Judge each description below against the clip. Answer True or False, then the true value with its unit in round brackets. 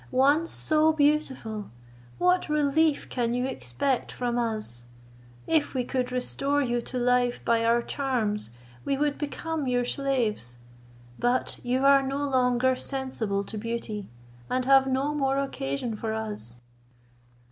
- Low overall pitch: False (255 Hz)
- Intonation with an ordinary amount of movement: True (3.2 semitones)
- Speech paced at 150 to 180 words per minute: False (135 wpm)